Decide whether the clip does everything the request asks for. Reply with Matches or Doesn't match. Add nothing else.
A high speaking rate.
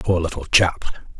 Doesn't match